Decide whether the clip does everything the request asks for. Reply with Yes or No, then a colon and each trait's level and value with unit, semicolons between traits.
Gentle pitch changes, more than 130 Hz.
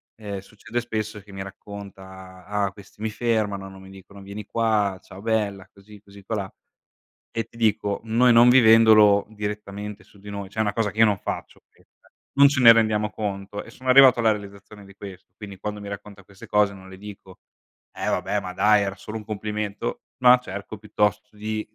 No: narrow, 1.7 semitones; low, 105 Hz